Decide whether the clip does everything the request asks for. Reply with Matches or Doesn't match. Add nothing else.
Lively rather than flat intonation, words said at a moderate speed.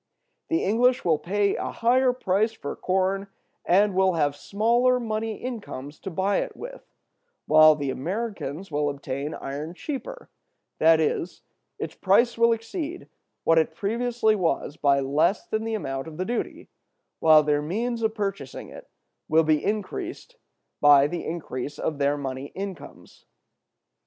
Matches